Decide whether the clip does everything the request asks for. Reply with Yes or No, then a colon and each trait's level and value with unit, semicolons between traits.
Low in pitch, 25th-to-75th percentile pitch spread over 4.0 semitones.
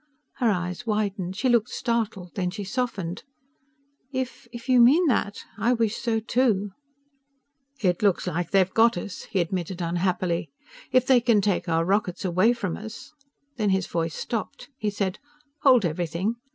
No: high, 205 Hz; average, 4.6 semitones